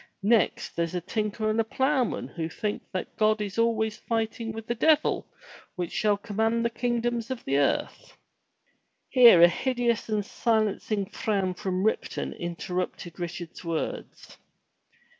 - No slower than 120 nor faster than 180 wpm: Yes, average, 150 wpm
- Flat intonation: No, average, 4.0 semitones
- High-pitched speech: Yes, high, 215 Hz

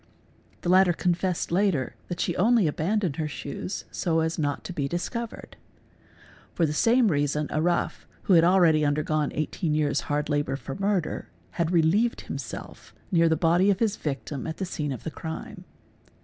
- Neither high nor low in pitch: Yes, medium, 165 Hz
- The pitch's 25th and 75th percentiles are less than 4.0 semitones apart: Yes, average, 3.6 semitones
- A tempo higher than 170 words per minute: Yes, average, 185 wpm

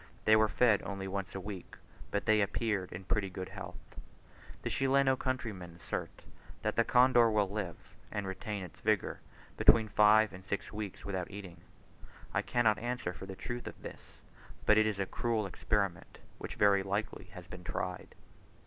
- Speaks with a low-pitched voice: Yes, low, 100 Hz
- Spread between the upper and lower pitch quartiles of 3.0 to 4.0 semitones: No, narrow, 2.5 semitones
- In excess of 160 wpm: Yes, average, 175 wpm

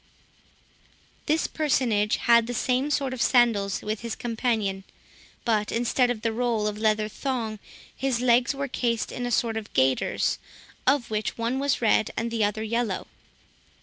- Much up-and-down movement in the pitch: No, narrow, 2.5 semitones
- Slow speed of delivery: No, average, 160 wpm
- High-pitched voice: Yes, high, 235 Hz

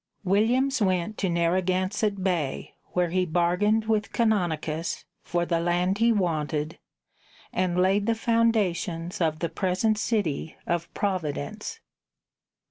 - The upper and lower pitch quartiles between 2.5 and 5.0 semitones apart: Yes, average, 3.7 semitones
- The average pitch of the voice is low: No, medium, 185 Hz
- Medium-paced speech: No, slow, 120 wpm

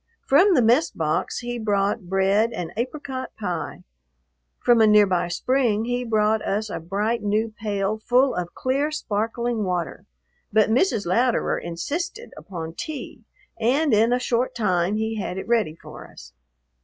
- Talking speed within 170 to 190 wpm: No, average, 155 wpm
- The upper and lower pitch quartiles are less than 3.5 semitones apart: No, average, 3.9 semitones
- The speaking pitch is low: No, high, 220 Hz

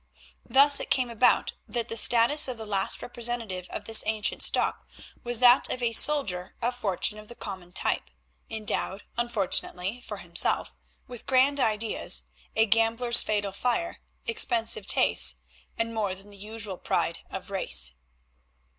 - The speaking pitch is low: No, high, 225 Hz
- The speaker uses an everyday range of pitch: Yes, average, 3.0 semitones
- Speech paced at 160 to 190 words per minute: No, average, 150 wpm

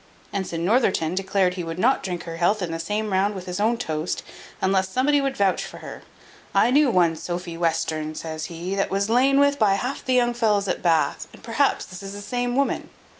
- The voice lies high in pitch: Yes, high, 195 Hz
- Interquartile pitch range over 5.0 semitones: Yes, wide, 5.5 semitones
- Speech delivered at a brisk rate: Yes, fast, 220 wpm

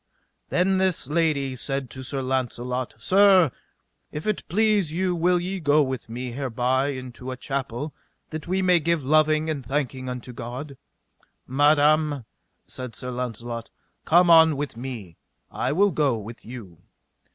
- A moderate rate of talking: Yes, average, 150 wpm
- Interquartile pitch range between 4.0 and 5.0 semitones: Yes, average, 4.3 semitones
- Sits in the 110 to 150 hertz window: Yes, medium, 140 Hz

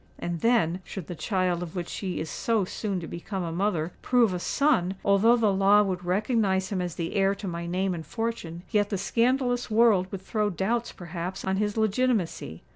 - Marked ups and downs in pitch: No, average, 3.7 semitones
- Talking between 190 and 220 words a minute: Yes, average, 195 wpm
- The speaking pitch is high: Yes, high, 195 Hz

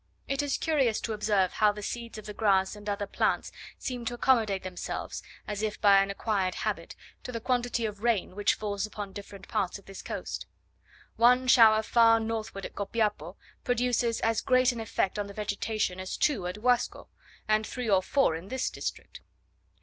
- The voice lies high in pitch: Yes, high, 215 Hz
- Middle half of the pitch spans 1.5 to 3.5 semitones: Yes, average, 3.0 semitones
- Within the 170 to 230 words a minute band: Yes, average, 190 wpm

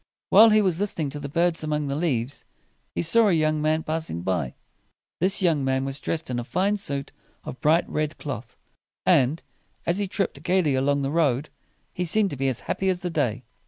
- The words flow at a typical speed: No, fast, 215 wpm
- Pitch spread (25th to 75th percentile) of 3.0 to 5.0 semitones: Yes, average, 4.5 semitones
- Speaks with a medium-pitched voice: Yes, medium, 155 Hz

